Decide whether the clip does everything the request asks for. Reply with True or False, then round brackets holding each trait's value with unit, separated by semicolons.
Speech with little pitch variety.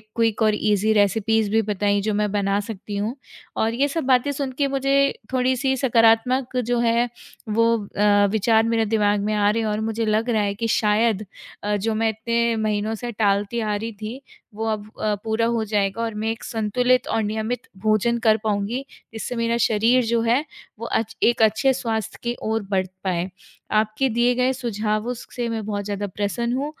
True (2.2 semitones)